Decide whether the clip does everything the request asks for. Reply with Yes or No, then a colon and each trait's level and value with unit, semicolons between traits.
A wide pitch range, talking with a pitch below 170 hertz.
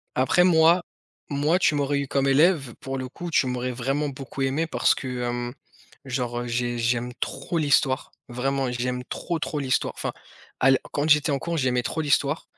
No: average, 3.1 semitones; low, 135 Hz